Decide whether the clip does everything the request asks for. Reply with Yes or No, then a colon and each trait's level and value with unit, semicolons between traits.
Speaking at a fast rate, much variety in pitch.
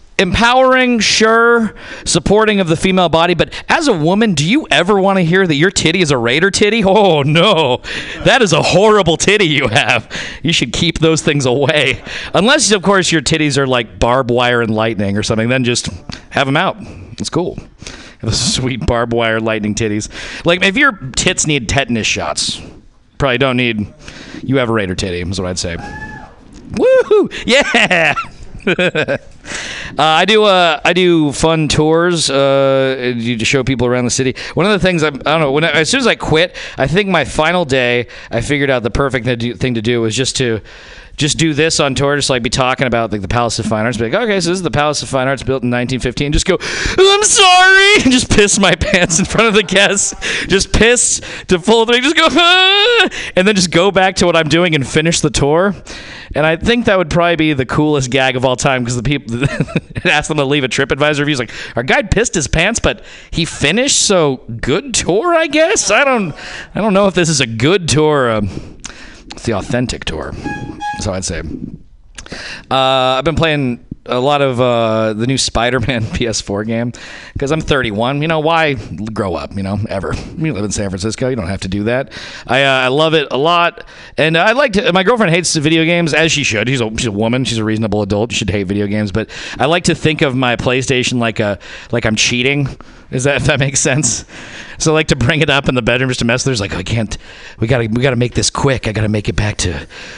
Yes: fast, 230 wpm; wide, 6.6 semitones